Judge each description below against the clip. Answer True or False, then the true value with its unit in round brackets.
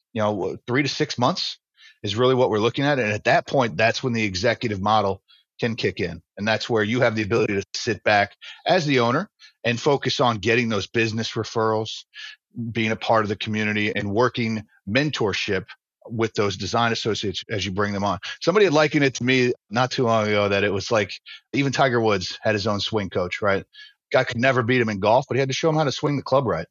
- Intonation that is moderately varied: True (3.4 semitones)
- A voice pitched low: True (115 Hz)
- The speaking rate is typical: False (235 wpm)